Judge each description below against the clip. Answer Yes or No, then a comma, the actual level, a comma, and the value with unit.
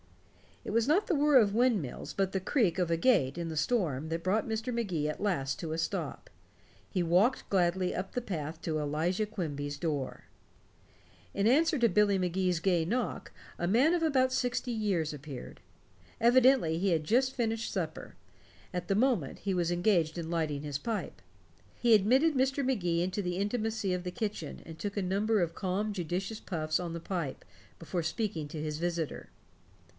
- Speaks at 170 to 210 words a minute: Yes, average, 180 wpm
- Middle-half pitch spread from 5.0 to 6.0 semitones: Yes, wide, 5.4 semitones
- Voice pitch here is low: No, medium, 185 Hz